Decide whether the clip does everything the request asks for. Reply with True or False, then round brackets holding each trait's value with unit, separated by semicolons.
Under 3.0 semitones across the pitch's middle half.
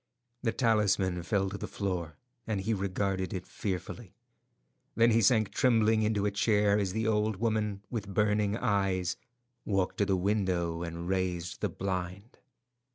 True (2.6 semitones)